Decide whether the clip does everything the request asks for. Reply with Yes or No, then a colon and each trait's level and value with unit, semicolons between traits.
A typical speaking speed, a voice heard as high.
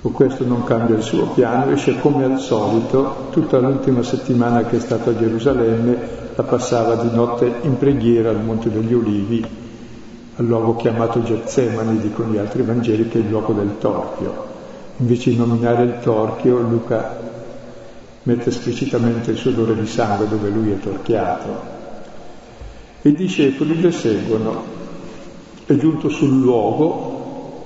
No: average, 150 wpm; low, 120 Hz